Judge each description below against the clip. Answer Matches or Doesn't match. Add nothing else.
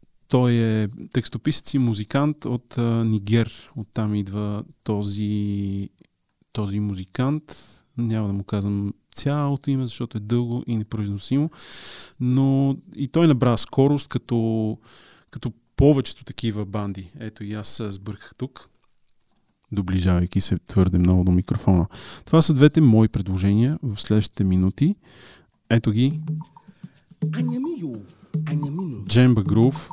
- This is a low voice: Matches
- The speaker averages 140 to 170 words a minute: Doesn't match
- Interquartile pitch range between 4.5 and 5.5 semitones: Matches